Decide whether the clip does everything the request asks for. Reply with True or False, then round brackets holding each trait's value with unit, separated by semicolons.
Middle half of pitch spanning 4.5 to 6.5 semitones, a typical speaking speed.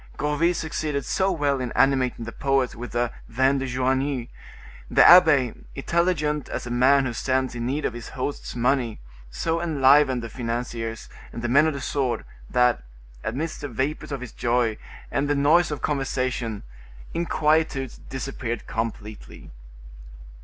False (3.4 semitones; 155 wpm)